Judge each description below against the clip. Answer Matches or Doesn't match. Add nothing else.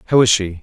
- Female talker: Doesn't match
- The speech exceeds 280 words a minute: Matches